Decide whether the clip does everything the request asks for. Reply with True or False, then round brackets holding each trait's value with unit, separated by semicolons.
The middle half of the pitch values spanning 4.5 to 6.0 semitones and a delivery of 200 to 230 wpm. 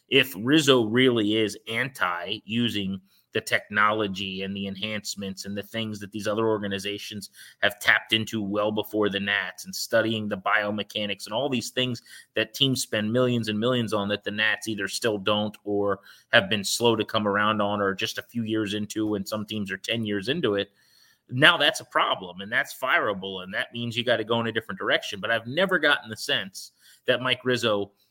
False (2.5 semitones; 205 wpm)